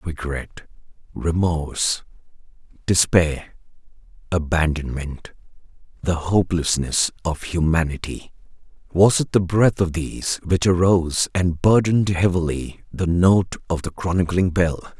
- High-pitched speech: No, very low, 85 Hz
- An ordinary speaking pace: No, slow, 95 wpm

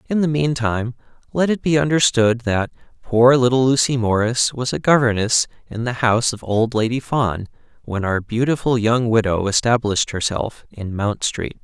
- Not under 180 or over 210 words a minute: No, average, 165 wpm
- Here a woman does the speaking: No, male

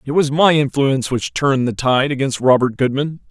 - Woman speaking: No, male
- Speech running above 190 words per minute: Yes, average, 200 wpm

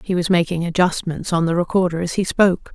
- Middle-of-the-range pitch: Yes, medium, 175 Hz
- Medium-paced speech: No, fast, 220 wpm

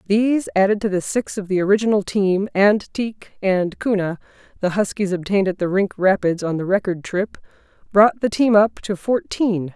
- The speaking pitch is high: Yes, high, 200 Hz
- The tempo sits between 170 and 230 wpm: Yes, average, 185 wpm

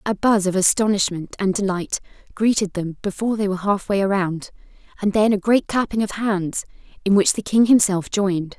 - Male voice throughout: No, female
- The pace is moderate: Yes, average, 190 wpm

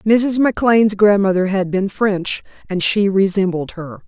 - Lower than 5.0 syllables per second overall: Yes, 4.5 syllables/s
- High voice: Yes, high, 200 Hz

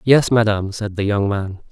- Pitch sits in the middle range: No, low, 105 Hz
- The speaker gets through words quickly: Yes, fast, 210 wpm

